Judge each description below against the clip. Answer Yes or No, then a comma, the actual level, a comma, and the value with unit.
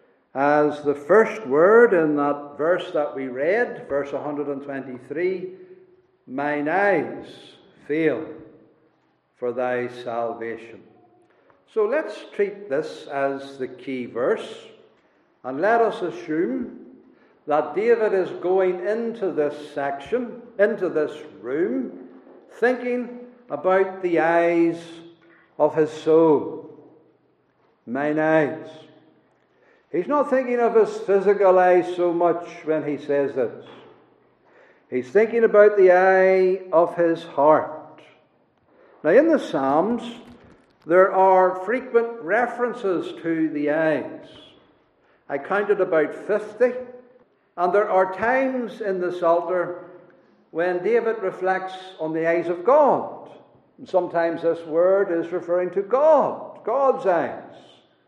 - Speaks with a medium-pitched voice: Yes, medium, 180 Hz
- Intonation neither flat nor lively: No, wide, 6.8 semitones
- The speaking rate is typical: No, slow, 115 wpm